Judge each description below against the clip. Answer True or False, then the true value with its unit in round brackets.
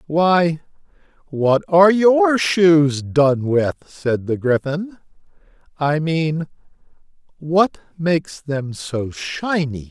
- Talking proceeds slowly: True (105 wpm)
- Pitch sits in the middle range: True (160 Hz)